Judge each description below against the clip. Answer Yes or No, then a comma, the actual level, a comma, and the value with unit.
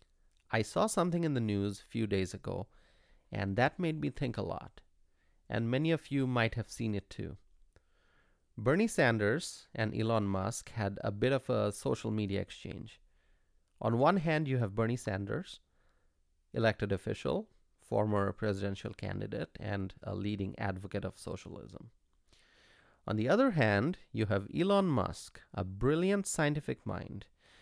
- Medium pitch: No, low, 105 Hz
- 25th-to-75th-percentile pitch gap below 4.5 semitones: No, average, 4.8 semitones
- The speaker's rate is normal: Yes, average, 150 wpm